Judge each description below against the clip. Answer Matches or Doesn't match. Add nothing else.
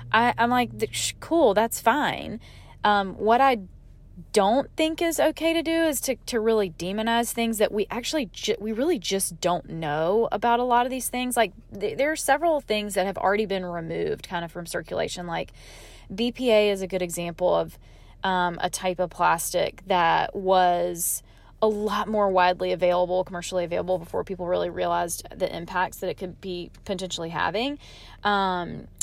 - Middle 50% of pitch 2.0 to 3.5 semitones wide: Doesn't match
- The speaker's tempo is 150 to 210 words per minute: Matches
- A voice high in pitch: Matches